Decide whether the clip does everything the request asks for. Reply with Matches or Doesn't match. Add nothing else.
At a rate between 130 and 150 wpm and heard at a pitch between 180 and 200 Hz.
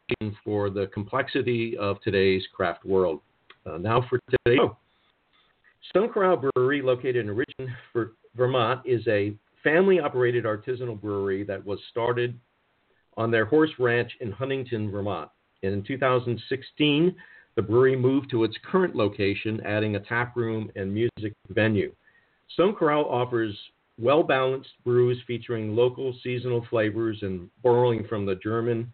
Doesn't match